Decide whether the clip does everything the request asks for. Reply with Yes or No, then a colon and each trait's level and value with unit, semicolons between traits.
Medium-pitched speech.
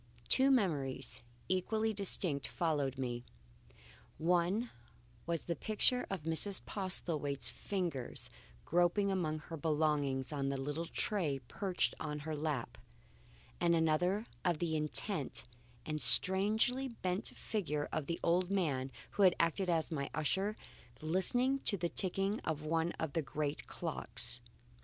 Yes: medium, 170 Hz